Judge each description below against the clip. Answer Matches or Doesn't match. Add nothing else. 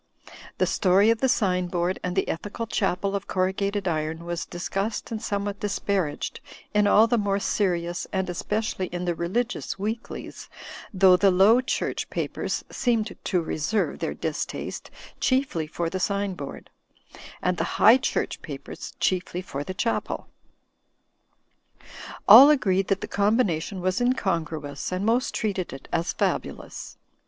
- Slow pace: Doesn't match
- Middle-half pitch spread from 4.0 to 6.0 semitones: Doesn't match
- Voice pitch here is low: Doesn't match